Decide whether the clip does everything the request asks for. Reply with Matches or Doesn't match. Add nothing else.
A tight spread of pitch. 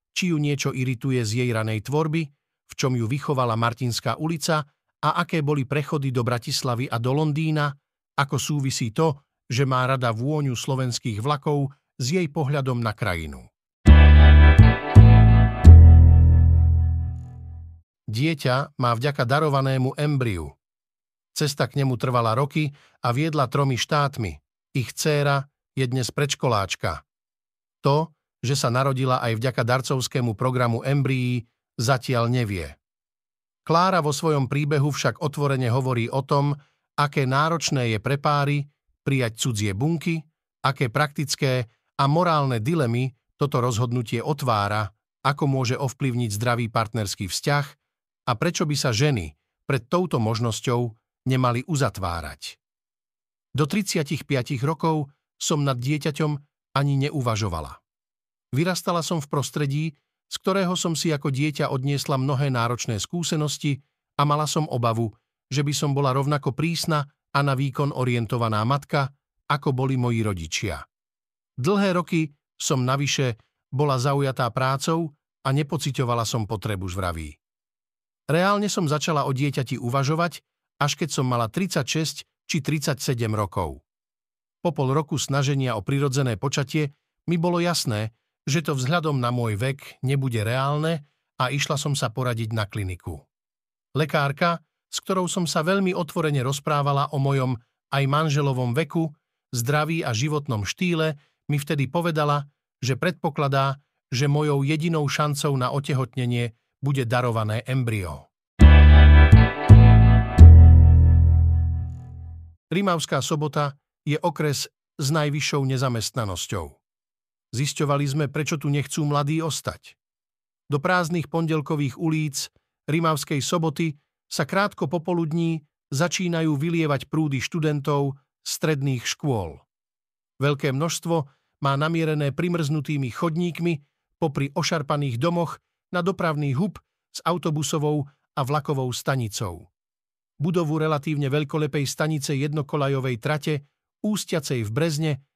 Doesn't match